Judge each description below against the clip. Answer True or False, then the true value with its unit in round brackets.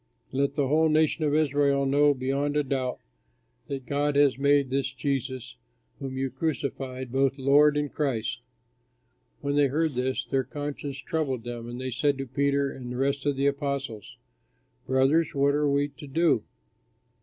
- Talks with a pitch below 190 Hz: True (140 Hz)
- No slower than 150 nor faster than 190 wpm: True (165 wpm)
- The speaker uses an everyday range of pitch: False (1.7 semitones)